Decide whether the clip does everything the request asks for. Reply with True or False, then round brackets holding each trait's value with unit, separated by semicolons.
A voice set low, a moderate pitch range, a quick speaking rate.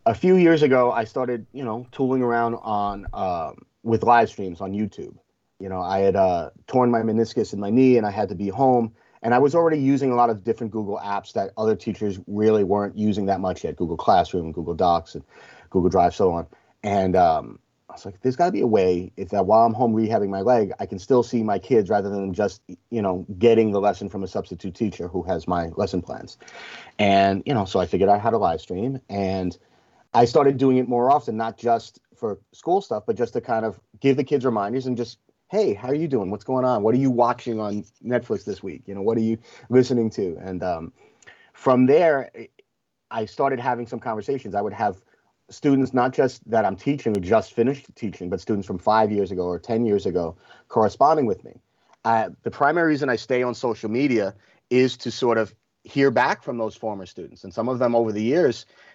True (115 Hz; 3.9 semitones; 230 wpm)